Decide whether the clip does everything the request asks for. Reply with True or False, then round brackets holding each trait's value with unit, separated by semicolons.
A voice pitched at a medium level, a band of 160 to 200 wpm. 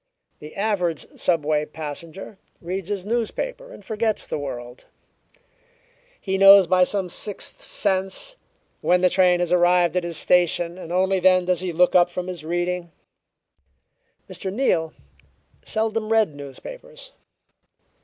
False (180 Hz; 135 wpm)